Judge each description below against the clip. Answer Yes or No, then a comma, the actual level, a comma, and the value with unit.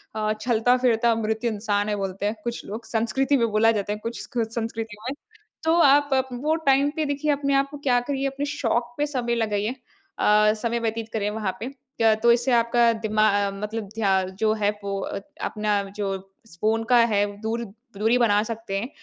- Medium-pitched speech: No, high, 225 Hz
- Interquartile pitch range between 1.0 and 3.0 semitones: Yes, narrow, 2.5 semitones